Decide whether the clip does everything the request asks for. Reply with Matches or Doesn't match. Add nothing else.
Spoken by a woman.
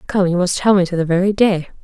Matches